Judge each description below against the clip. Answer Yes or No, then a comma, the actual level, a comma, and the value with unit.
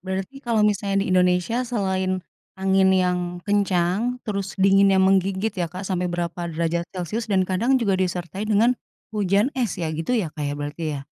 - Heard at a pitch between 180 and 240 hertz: Yes, high, 190 Hz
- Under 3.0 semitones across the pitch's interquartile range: Yes, narrow, 2.5 semitones